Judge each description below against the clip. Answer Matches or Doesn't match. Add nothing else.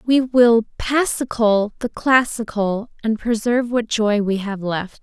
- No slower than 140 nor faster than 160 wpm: Matches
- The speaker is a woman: Matches